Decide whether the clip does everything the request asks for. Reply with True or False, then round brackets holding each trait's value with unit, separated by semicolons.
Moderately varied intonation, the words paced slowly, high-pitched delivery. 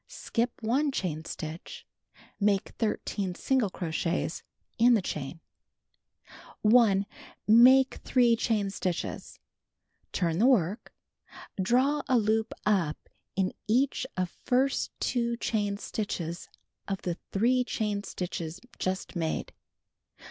True (4.9 semitones; 110 wpm; 210 Hz)